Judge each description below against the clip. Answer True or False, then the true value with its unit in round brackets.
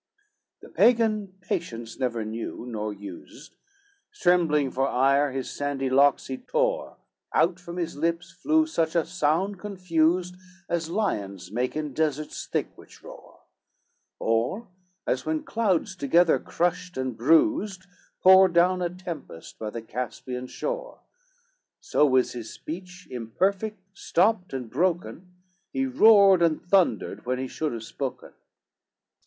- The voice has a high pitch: False (165 Hz)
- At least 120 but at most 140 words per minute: True (135 wpm)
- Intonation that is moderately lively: False (6.3 semitones)